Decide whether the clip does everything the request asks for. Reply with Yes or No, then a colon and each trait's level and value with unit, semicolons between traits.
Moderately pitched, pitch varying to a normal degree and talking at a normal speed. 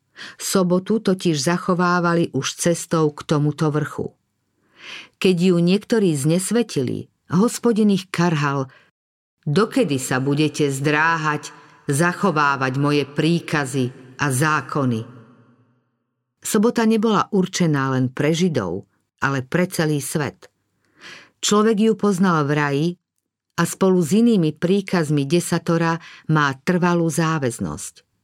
No: medium, 160 Hz; average, 4.6 semitones; slow, 100 wpm